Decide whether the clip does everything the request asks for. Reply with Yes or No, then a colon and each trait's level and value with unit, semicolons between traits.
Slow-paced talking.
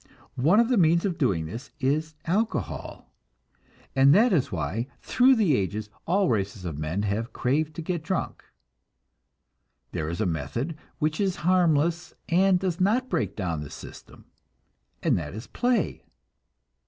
No: average, 155 wpm